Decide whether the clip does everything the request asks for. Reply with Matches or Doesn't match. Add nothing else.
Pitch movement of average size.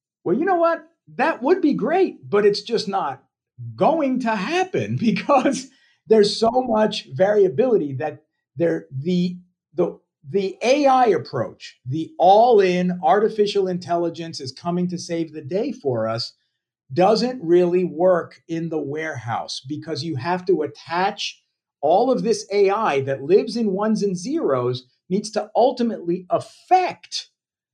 Doesn't match